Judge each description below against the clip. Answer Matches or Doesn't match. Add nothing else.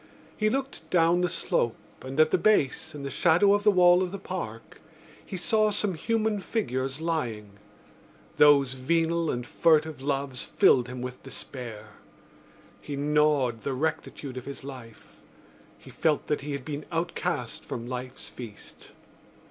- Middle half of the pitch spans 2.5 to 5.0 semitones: Doesn't match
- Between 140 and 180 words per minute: Matches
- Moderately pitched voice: Matches